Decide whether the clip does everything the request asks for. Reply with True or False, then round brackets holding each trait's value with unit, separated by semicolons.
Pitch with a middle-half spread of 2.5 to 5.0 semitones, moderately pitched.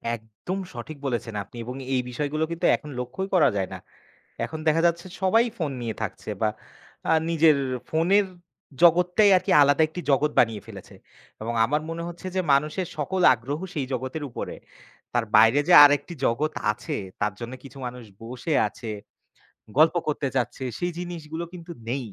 False (5.6 semitones; 145 Hz)